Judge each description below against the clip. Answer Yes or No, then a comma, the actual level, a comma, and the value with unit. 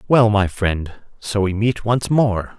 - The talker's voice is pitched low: Yes, low, 105 Hz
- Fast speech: No, average, 185 wpm